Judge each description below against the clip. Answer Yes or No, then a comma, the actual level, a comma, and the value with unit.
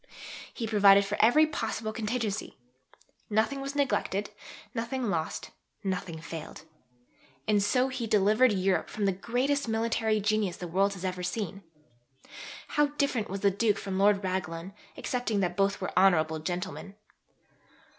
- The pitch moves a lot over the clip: No, average, 3.3 semitones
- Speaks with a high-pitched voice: Yes, high, 205 Hz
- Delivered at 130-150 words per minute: Yes, slow, 135 wpm